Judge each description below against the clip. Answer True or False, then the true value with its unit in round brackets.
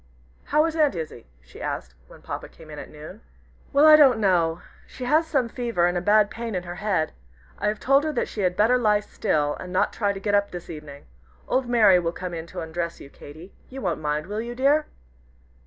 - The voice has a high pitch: True (200 Hz)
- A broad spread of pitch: True (6.3 semitones)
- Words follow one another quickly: True (230 wpm)